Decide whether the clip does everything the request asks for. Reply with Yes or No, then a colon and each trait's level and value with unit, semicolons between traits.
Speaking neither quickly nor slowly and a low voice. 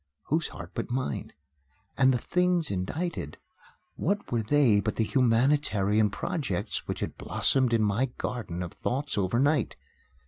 Yes: average, 145 wpm; low, 120 Hz